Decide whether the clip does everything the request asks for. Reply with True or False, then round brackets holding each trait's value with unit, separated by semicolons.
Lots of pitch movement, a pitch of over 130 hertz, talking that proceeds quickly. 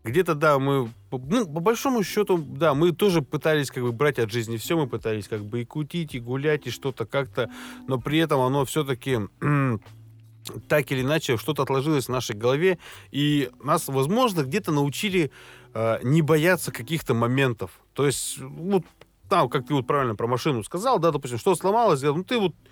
False (4.6 semitones; 140 Hz; 180 wpm)